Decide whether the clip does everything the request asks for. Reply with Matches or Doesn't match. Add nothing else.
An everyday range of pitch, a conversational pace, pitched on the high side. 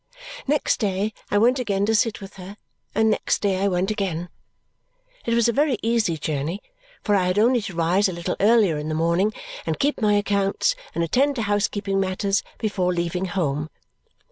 Matches